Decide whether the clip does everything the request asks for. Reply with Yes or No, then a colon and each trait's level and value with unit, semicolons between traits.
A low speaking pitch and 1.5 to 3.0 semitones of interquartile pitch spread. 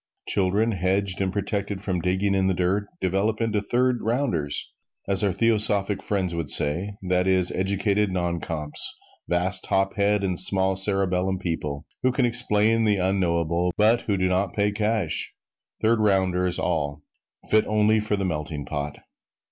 Yes: very low, 95 Hz; narrow, 2.5 semitones